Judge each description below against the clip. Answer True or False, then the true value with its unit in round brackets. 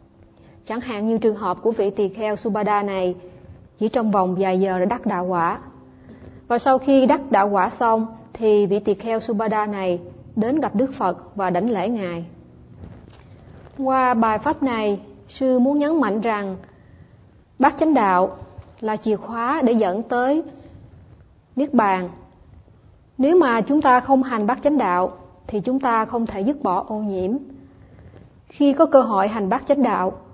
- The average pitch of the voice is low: False (225 Hz)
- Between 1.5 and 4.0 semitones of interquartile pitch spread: False (4.7 semitones)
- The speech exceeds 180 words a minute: False (170 wpm)